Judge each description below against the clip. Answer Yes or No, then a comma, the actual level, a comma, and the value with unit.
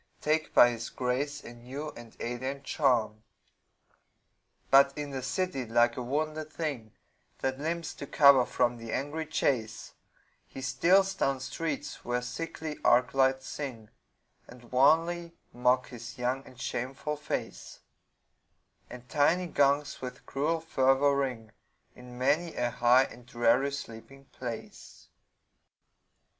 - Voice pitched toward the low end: Yes, low, 130 Hz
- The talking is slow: Yes, slow, 130 wpm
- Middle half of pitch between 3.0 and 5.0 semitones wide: Yes, average, 3.3 semitones